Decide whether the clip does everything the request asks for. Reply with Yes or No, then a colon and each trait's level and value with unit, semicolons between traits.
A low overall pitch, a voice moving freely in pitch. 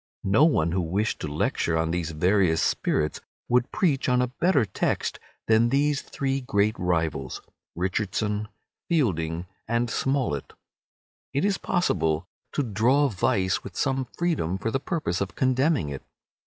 Yes: low, 105 Hz; wide, 7.6 semitones